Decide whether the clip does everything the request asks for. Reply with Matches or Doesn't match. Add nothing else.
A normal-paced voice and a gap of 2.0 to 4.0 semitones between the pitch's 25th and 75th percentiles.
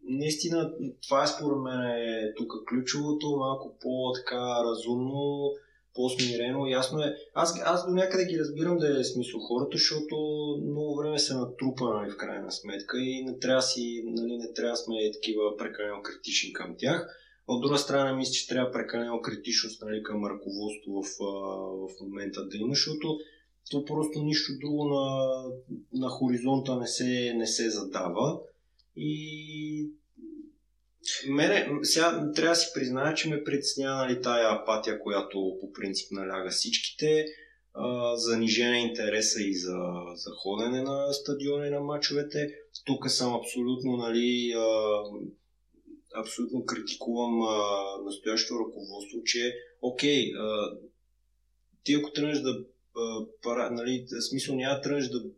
Doesn't match